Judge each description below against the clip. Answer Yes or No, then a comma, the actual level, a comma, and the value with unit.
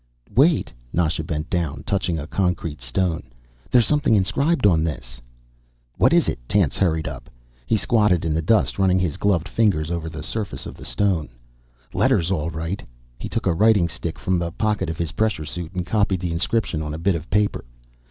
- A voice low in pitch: Yes, very low, 85 Hz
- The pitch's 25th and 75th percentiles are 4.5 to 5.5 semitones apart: No, average, 4.1 semitones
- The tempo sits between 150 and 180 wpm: No, average, 190 wpm